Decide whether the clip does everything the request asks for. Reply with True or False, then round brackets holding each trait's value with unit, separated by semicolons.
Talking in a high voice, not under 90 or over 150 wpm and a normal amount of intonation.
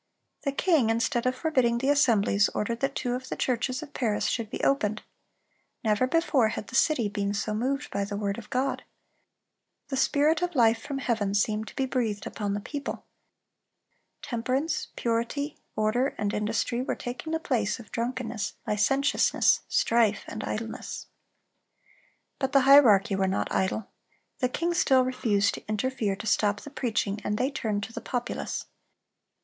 False (235 Hz; 165 wpm; 4.1 semitones)